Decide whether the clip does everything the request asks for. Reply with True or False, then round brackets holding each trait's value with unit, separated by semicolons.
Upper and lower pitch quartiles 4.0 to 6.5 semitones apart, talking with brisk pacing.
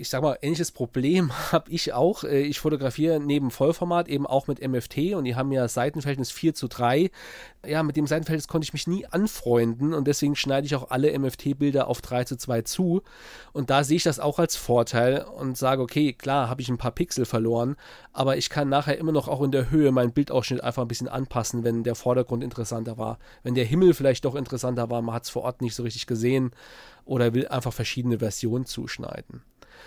False (3.2 semitones; 215 wpm)